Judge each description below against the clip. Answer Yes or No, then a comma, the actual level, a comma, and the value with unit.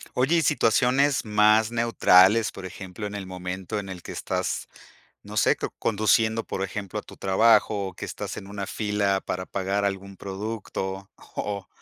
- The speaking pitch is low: Yes, low, 100 Hz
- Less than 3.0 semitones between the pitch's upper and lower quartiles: Yes, narrow, 2.4 semitones